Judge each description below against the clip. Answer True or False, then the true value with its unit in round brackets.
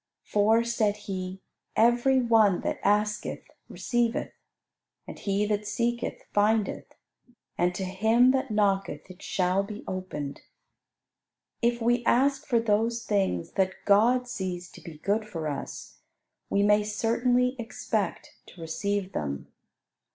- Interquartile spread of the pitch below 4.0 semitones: True (3.6 semitones)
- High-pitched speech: True (210 Hz)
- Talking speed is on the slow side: True (130 wpm)